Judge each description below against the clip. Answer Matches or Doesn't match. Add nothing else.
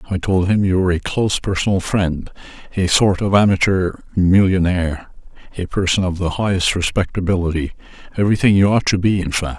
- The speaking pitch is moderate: Doesn't match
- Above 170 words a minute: Doesn't match